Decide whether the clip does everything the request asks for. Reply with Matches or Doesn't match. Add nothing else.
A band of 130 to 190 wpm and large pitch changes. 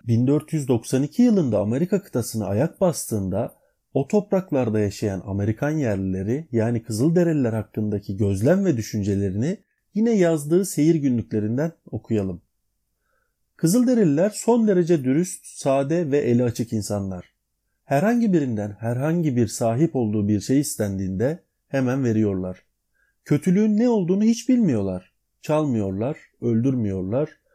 Doesn't match